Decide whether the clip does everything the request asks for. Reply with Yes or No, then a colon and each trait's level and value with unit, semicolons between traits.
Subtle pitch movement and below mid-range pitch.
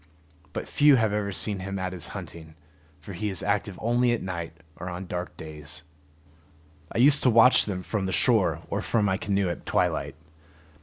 No: average, 3.5 semitones; low, 100 Hz